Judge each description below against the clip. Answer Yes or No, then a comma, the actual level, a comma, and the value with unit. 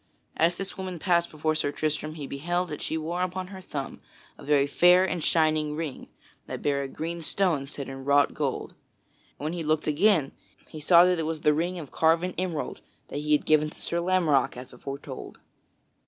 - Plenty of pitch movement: No, average, 3.2 semitones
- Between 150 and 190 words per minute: No, average, 200 wpm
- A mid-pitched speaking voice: Yes, medium, 155 Hz